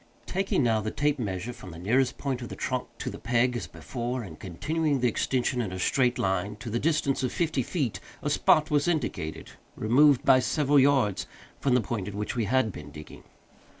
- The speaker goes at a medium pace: No, fast, 210 wpm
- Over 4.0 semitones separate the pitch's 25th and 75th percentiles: Yes, average, 4.7 semitones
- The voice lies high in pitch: No, low, 125 Hz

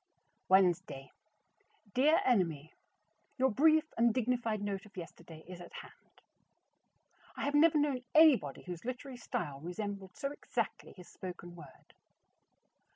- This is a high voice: Yes, high, 205 Hz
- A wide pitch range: Yes, wide, 7.0 semitones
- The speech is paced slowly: Yes, slow, 125 wpm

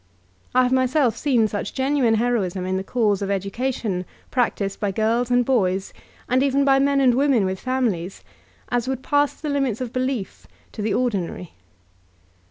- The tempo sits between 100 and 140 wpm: No, average, 180 wpm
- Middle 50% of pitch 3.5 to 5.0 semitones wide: Yes, average, 4.7 semitones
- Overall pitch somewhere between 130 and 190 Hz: No, high, 245 Hz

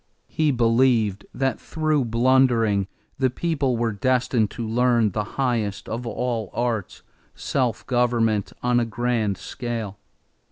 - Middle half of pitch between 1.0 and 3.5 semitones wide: Yes, narrow, 2.5 semitones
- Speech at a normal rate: No, slow, 125 wpm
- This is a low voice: Yes, low, 120 Hz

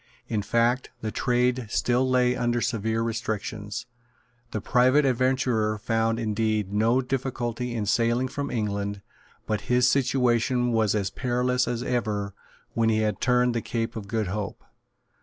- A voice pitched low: Yes, low, 115 Hz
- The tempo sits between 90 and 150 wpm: Yes, average, 145 wpm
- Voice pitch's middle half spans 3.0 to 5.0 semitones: No, narrow, 2.5 semitones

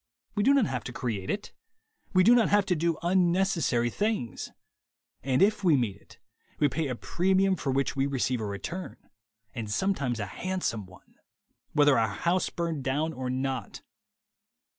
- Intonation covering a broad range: Yes, wide, 7.0 semitones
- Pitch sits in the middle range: Yes, medium, 145 Hz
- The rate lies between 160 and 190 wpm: Yes, average, 175 wpm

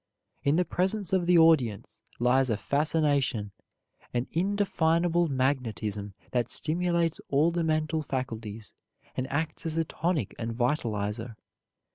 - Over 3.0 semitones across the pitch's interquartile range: Yes, wide, 5.5 semitones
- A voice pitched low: No, medium, 145 Hz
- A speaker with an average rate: No, slow, 125 wpm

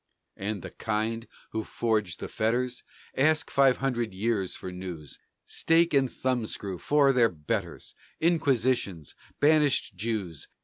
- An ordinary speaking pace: No, slow, 125 wpm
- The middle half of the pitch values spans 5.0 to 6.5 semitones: Yes, wide, 5.6 semitones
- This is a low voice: Yes, low, 115 Hz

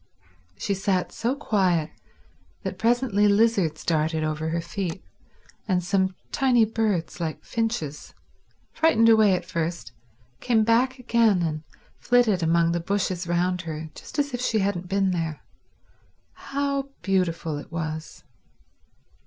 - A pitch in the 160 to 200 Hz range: Yes, high, 190 Hz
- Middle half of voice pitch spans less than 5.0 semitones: No, average, 5.3 semitones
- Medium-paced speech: No, slow, 130 wpm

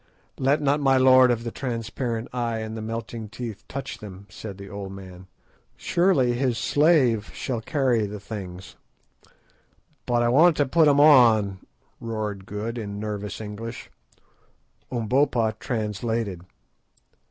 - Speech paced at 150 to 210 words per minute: No, slow, 135 wpm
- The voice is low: Yes, low, 115 Hz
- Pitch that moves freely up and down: No, average, 3.7 semitones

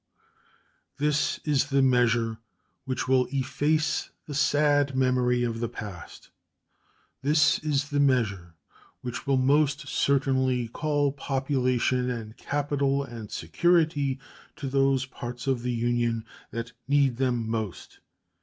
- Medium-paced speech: No, slow, 120 wpm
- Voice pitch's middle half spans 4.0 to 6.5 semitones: No, average, 3.0 semitones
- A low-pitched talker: Yes, low, 130 Hz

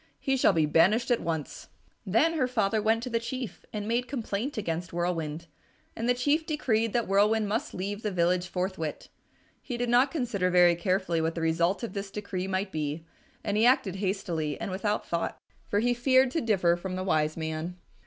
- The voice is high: Yes, high, 200 Hz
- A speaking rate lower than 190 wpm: No, average, 195 wpm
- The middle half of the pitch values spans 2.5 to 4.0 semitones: No, average, 5.2 semitones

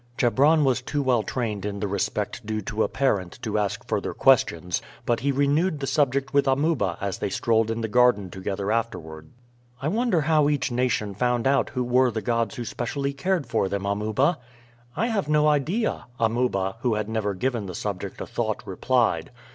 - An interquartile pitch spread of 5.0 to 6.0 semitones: Yes, average, 5.3 semitones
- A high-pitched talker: No, low, 120 Hz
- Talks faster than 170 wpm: Yes, average, 190 wpm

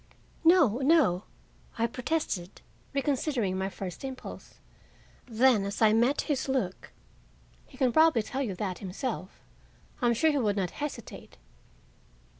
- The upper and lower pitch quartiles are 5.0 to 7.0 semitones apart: Yes, wide, 5.6 semitones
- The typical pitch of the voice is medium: No, high, 240 Hz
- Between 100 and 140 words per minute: Yes, slow, 135 wpm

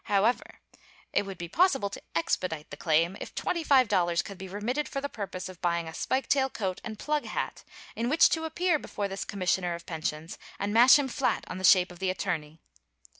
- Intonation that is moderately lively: No, wide, 7.0 semitones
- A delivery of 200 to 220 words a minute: Yes, fast, 205 wpm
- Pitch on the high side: Yes, high, 195 Hz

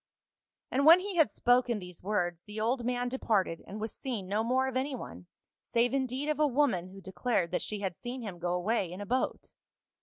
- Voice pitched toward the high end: Yes, high, 230 Hz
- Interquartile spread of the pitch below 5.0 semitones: No, wide, 5.4 semitones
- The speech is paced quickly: Yes, fast, 225 wpm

